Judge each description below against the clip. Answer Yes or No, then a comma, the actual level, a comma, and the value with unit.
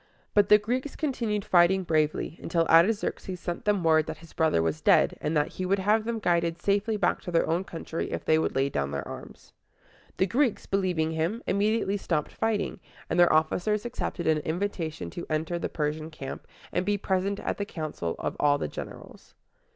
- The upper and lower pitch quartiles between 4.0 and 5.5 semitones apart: Yes, average, 4.4 semitones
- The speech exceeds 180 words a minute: Yes, average, 195 wpm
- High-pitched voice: No, medium, 175 Hz